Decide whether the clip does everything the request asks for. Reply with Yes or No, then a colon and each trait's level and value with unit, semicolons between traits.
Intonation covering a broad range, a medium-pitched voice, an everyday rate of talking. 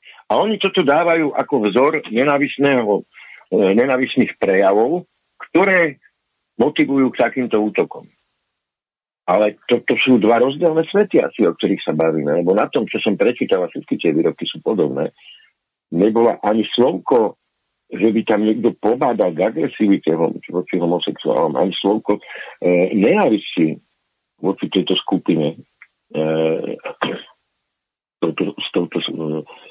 No: wide, 5.9 semitones; low, 110 Hz; average, 130 wpm